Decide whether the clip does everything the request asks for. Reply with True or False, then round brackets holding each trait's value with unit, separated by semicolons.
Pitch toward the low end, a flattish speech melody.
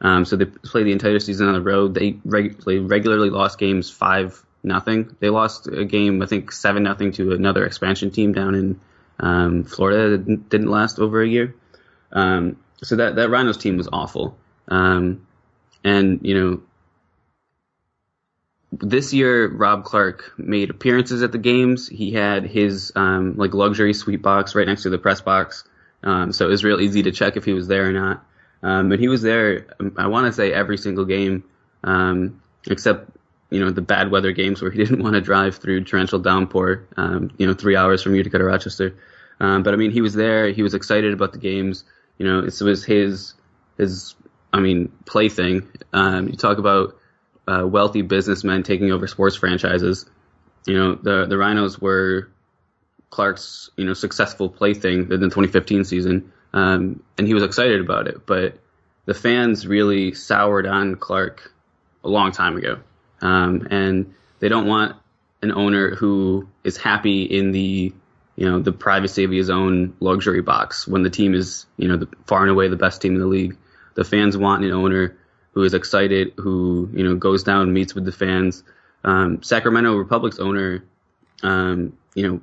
True (95 Hz; 1.7 semitones)